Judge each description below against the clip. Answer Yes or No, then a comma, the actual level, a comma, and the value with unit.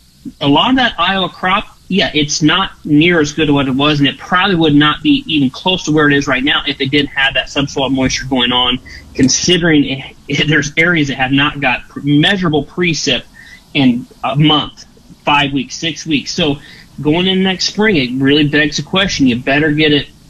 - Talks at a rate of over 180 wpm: Yes, fast, 205 wpm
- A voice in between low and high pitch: Yes, medium, 150 Hz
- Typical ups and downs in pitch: Yes, average, 3.9 semitones